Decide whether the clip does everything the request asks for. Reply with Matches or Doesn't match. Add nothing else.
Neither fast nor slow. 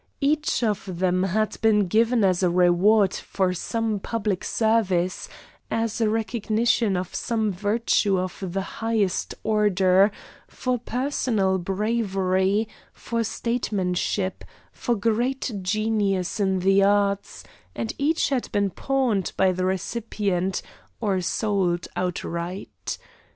Doesn't match